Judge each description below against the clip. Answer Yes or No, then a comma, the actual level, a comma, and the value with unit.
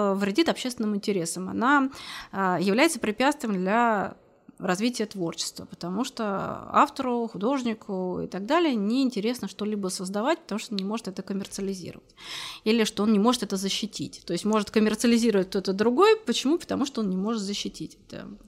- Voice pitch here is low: No, high, 215 Hz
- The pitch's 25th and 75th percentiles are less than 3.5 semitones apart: No, average, 3.8 semitones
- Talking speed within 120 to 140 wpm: No, average, 155 wpm